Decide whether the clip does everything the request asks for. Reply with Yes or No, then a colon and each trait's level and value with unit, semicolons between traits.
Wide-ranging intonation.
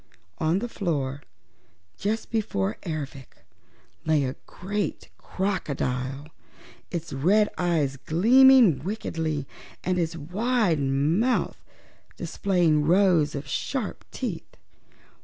Yes: wide, 5.8 semitones